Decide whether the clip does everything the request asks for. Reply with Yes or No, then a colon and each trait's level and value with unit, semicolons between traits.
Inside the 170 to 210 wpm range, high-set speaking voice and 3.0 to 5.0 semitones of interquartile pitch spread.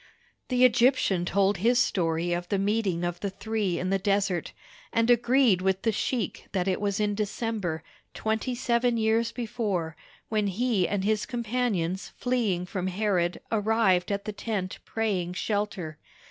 No: average, 155 wpm; high, 205 Hz; average, 3.6 semitones